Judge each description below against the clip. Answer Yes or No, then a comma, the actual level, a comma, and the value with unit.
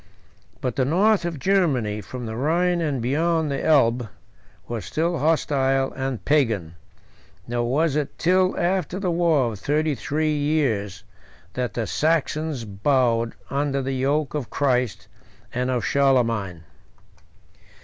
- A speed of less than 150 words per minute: Yes, slow, 135 wpm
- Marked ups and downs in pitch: No, average, 4.7 semitones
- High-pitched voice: No, medium, 140 Hz